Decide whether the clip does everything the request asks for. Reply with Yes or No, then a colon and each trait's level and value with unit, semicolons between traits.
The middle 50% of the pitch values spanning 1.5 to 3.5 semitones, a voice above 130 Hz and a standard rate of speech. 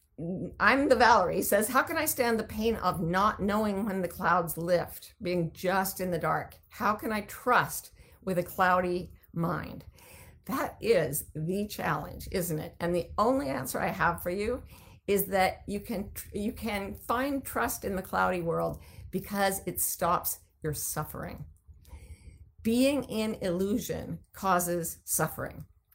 No: average, 4.2 semitones; medium, 185 Hz; average, 155 wpm